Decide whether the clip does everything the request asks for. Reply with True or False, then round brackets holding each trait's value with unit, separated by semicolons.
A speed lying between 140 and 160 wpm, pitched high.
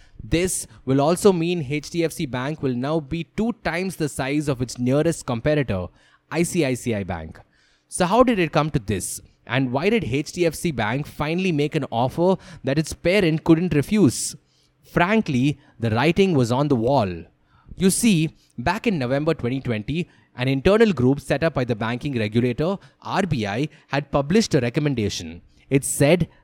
False (155 wpm; 145 Hz)